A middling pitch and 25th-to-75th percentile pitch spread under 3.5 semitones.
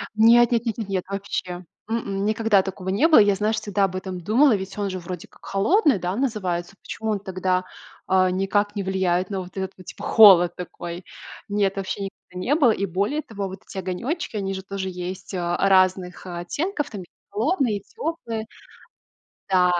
No: high, 195 Hz; average, 2.9 semitones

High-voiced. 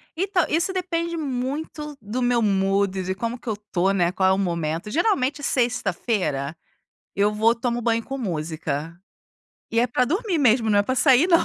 Yes: high, 235 Hz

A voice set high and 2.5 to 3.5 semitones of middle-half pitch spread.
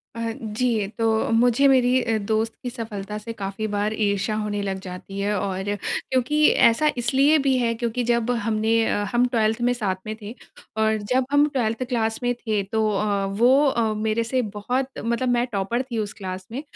Yes: high, 225 Hz; average, 2.8 semitones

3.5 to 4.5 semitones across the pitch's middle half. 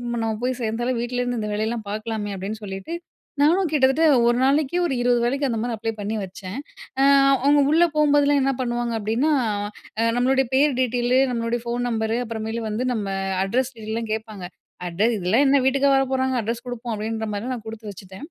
No: average, 3.1 semitones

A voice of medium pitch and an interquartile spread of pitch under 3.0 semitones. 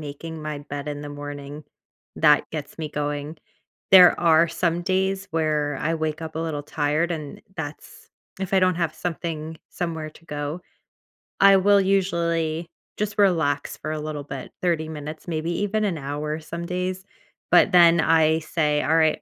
Yes: medium, 160 Hz; narrow, 2.6 semitones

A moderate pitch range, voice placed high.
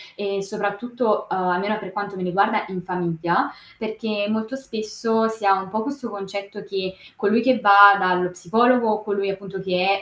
No: narrow, 2.3 semitones; high, 200 Hz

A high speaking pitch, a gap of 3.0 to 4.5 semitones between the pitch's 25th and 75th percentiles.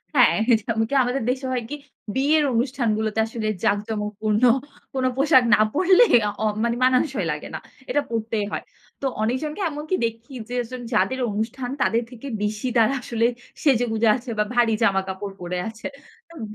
Yes: high, 235 Hz; average, 3.3 semitones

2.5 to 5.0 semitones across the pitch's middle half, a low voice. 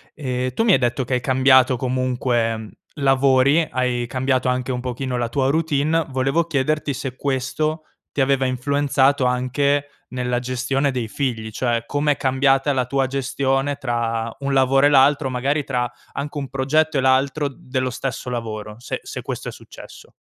No: narrow, 1.9 semitones; low, 130 Hz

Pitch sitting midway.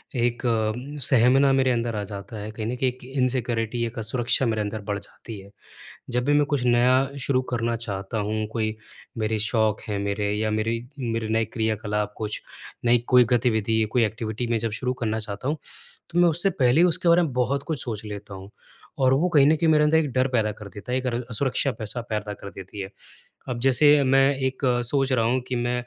No: low, 120 Hz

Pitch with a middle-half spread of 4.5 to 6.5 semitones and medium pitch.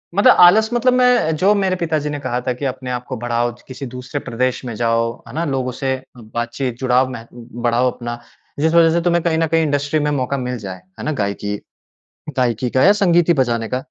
No: average, 5.0 semitones; low, 130 Hz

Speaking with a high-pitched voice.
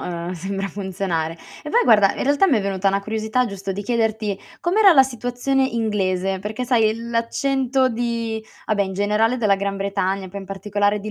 Yes: high, 210 Hz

